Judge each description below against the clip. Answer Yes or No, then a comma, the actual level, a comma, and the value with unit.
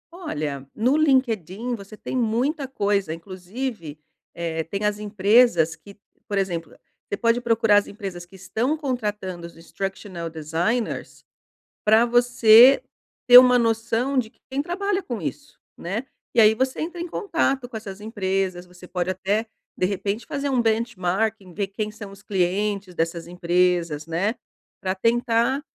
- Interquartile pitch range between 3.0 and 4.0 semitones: No, average, 4.9 semitones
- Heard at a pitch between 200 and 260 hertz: Yes, high, 210 Hz